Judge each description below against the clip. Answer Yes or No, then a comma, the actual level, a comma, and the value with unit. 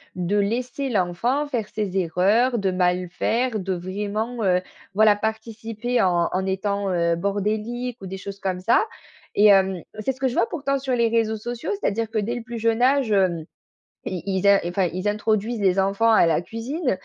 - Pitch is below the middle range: No, high, 210 Hz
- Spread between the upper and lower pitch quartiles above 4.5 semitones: No, average, 3.7 semitones